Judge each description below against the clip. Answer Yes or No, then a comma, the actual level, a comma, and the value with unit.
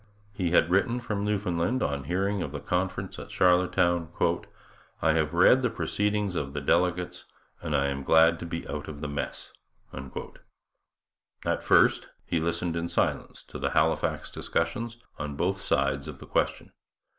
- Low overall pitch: Yes, very low, 85 Hz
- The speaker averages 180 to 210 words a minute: No, average, 160 wpm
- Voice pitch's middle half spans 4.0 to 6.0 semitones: Yes, average, 4.3 semitones